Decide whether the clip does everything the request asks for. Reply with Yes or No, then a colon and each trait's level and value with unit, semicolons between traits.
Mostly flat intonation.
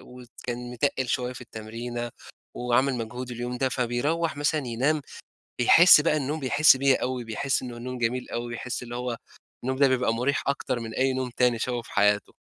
Yes: narrow, 1.9 semitones